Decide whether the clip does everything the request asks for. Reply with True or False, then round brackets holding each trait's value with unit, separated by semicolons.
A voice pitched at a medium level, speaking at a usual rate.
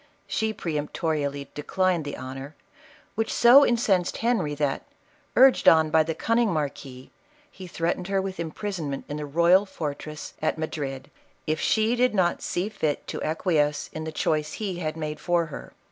True (160 Hz; 160 wpm)